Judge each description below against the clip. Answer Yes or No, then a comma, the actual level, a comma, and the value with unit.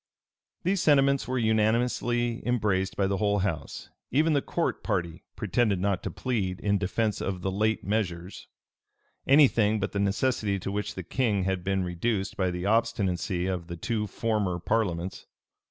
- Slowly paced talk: No, average, 170 wpm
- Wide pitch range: No, average, 3.6 semitones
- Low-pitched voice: Yes, low, 100 Hz